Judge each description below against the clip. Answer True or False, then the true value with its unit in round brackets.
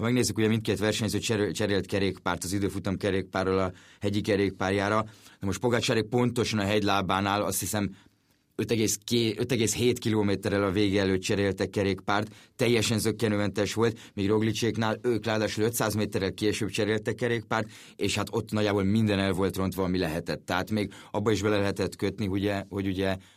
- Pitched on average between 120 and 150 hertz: False (105 Hz)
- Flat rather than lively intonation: True (2.0 semitones)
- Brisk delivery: True (160 wpm)